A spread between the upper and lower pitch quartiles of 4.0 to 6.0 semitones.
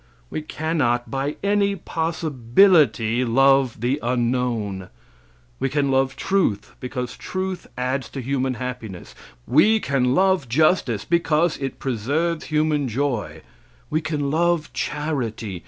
Yes: average, 4.5 semitones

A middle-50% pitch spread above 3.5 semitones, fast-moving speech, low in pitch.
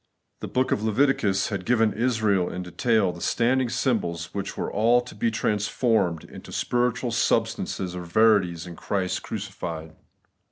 No: average, 4.5 semitones; average, 155 wpm; low, 105 Hz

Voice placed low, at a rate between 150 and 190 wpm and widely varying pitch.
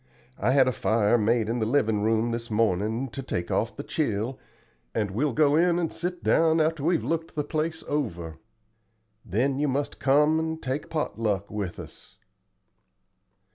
Yes: low, 130 Hz; average, 175 wpm; wide, 5.8 semitones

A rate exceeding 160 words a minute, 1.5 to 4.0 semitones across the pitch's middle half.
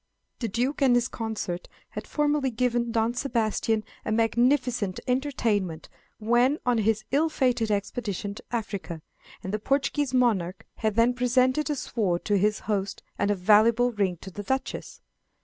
No: average, 155 wpm; average, 3.5 semitones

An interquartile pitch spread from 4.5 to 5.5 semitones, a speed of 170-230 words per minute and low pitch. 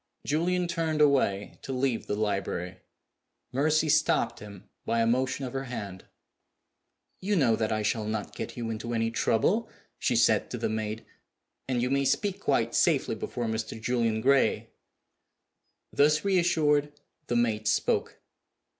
No: average, 5.2 semitones; average, 155 wpm; low, 125 Hz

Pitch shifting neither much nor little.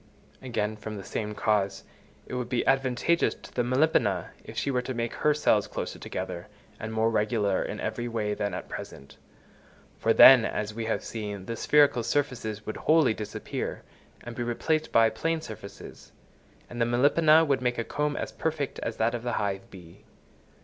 Yes: average, 3.8 semitones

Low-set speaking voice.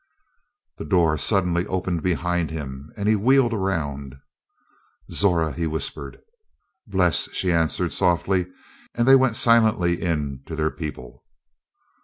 Yes: very low, 85 Hz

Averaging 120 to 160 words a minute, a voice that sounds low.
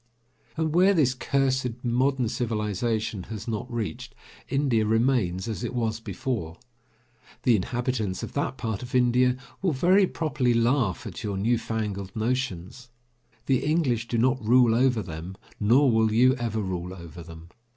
Yes: average, 150 wpm; low, 120 Hz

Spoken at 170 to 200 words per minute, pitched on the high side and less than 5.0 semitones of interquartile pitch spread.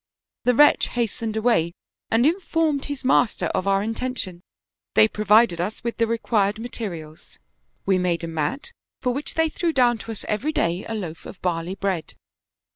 No: average, 175 wpm; high, 220 Hz; average, 5.3 semitones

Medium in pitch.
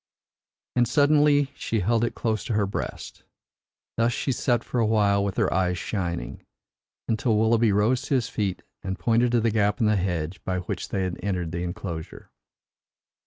No: low, 105 Hz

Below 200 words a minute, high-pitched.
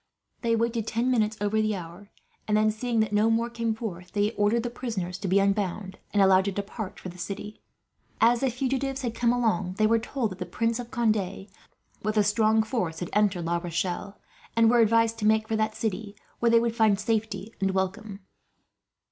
No: fast, 205 wpm; high, 215 Hz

